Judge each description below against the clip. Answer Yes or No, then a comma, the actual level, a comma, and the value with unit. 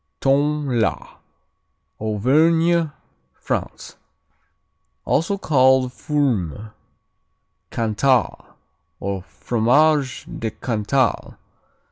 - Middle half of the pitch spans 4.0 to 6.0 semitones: Yes, average, 5.1 semitones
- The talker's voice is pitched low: Yes, low, 130 Hz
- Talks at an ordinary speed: No, slow, 60 wpm